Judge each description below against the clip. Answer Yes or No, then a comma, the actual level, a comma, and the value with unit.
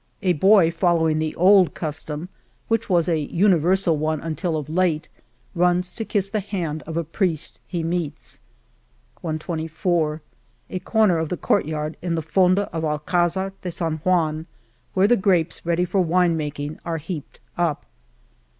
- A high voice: No, medium, 170 Hz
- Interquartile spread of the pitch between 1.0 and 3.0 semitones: Yes, narrow, 2.6 semitones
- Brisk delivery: No, average, 160 wpm